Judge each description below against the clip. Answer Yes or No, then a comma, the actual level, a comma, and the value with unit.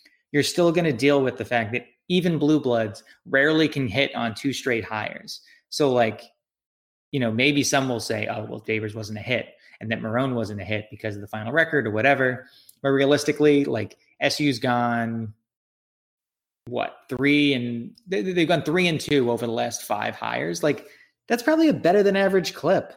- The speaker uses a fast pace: No, average, 195 wpm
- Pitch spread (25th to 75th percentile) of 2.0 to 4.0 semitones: No, average, 4.7 semitones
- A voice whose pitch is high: No, low, 135 Hz